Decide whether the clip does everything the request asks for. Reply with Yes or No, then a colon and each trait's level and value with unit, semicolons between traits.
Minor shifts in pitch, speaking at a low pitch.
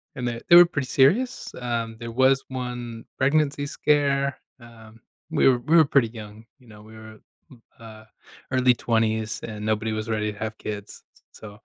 No: average, 3.6 semitones; low, 115 Hz